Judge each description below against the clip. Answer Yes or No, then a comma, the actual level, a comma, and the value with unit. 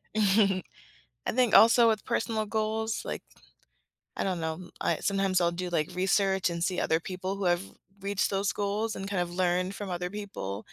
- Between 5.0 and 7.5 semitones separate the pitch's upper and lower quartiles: No, narrow, 2.6 semitones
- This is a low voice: No, high, 195 Hz